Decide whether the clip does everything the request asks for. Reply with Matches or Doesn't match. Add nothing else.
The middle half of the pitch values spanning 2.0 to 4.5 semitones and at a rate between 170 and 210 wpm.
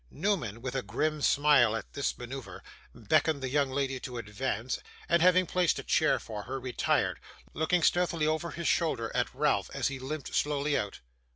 Matches